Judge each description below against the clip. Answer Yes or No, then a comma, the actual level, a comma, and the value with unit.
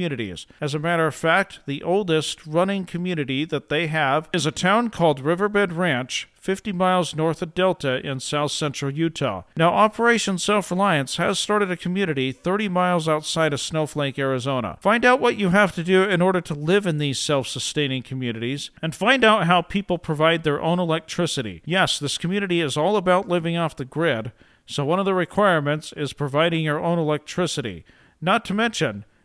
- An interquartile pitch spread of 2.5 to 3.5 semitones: No, average, 4.2 semitones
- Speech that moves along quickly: No, average, 185 wpm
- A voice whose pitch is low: No, medium, 165 Hz